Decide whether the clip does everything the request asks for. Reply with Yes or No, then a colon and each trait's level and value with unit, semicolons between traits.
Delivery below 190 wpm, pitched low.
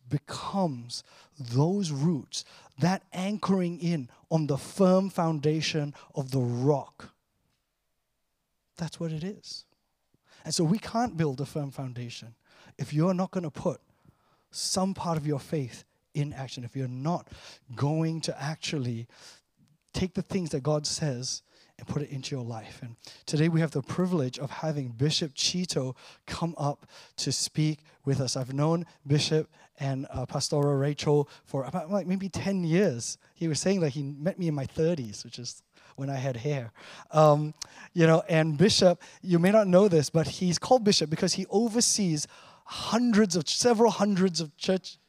No: average, 165 wpm; medium, 155 Hz